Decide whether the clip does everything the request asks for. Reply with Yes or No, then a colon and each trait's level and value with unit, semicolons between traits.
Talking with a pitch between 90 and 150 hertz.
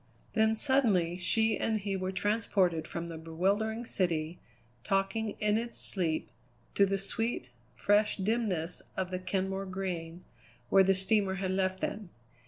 No: high, 195 Hz